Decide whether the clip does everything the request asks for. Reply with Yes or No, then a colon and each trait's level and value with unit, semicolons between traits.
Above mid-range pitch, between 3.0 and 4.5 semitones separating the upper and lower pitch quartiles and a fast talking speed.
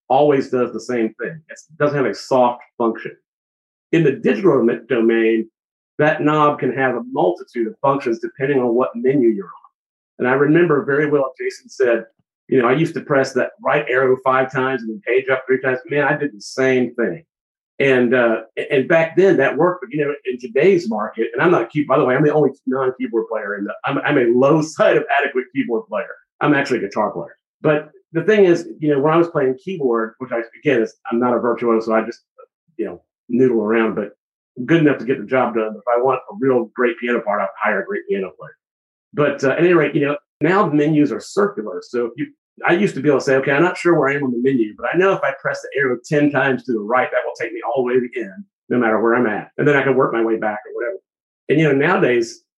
No: low, 130 Hz; average, 4.0 semitones; fast, 255 wpm